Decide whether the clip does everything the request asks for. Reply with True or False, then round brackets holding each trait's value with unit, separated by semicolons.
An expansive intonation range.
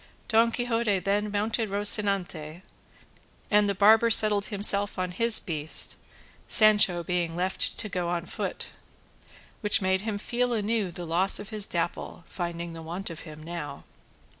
False (3.6 semitones)